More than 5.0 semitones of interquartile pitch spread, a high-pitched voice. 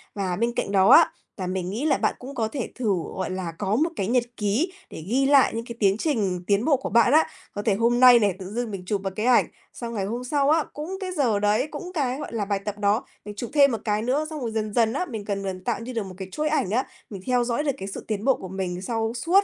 No: average, 4.7 semitones; high, 225 Hz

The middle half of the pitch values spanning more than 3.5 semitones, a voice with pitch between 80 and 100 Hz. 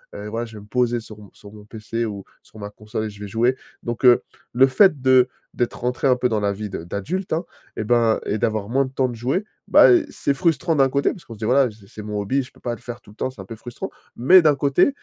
No: average, 3.9 semitones; low, 120 Hz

